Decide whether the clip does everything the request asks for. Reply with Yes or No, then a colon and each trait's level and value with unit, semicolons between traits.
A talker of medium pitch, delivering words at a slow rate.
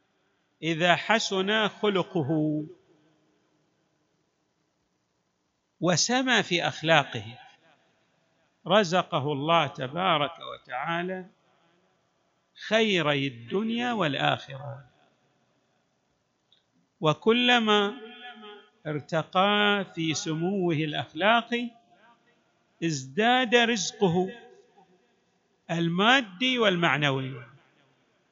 Yes: medium, 180 Hz; slow, 45 wpm